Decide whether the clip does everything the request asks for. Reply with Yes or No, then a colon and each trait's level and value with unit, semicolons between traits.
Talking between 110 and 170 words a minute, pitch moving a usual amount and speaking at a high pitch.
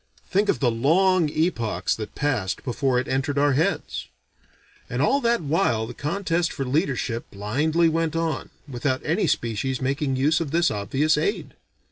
No: average, 160 wpm; average, 4.7 semitones; medium, 145 Hz